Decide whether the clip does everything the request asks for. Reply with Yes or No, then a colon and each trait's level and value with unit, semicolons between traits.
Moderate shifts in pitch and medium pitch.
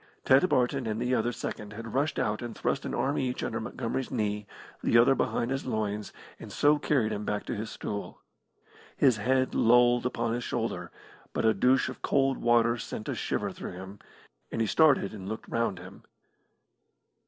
No: average, 3.4 semitones; low, 115 Hz